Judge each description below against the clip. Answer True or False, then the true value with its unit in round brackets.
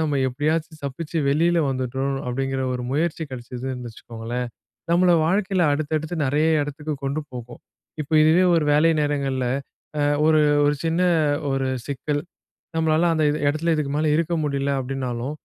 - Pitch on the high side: False (145 Hz)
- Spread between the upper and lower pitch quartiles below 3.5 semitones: True (3.1 semitones)